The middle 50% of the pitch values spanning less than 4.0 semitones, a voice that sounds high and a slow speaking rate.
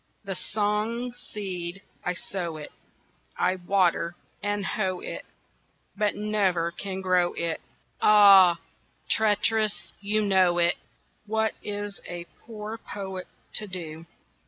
Yes: average, 3.0 semitones; high, 195 Hz; slow, 115 wpm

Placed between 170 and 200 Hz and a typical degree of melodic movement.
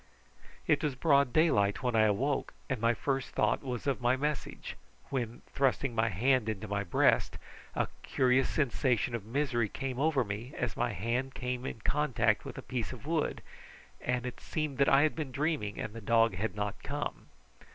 No: low, 125 Hz; average, 3.6 semitones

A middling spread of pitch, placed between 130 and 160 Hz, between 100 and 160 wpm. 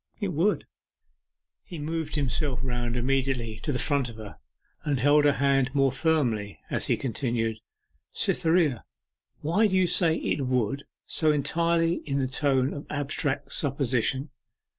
Yes: average, 3.6 semitones; medium, 140 Hz; average, 145 wpm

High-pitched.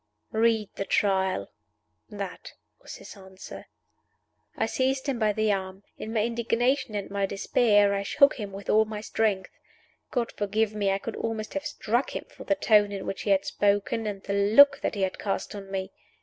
Yes: high, 210 Hz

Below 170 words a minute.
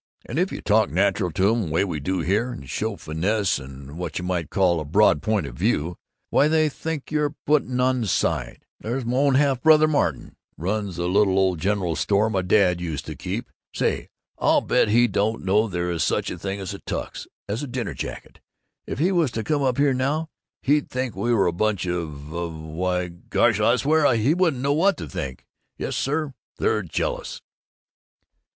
No: average, 200 wpm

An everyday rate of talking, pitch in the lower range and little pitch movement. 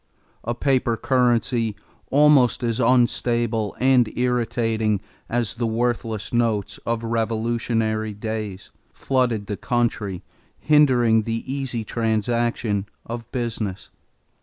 No: slow, 100 wpm; low, 115 Hz; narrow, 1.8 semitones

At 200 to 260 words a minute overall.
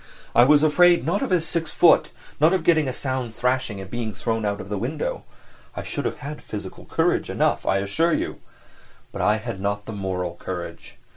Yes: fast, 205 wpm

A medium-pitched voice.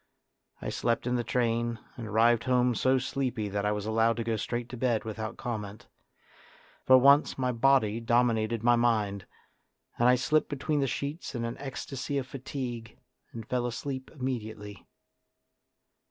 No: low, 120 Hz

